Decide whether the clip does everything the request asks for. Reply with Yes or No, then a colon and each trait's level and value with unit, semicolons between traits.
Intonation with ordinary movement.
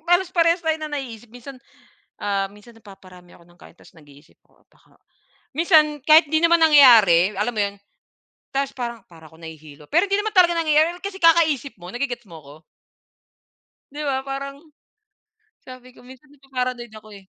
No: wide, 7.7 semitones